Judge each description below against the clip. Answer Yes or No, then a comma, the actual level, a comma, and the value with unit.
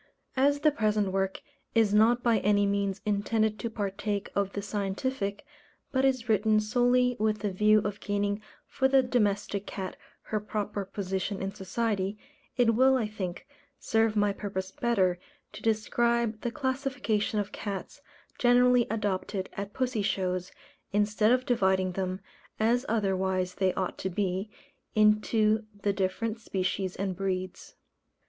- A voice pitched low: No, high, 210 Hz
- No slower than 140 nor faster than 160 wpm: Yes, average, 145 wpm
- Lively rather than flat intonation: No, average, 2.9 semitones